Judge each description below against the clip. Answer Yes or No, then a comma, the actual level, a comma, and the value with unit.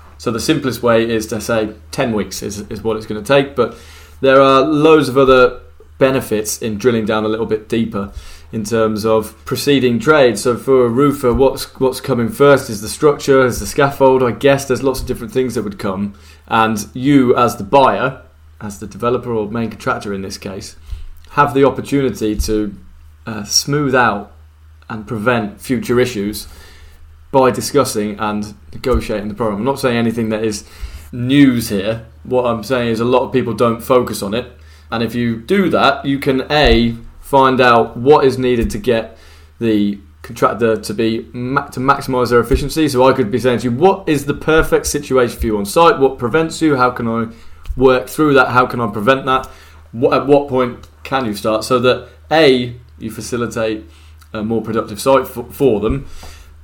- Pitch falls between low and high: No, low, 115 Hz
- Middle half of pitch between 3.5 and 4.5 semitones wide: Yes, average, 3.8 semitones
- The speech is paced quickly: No, average, 190 wpm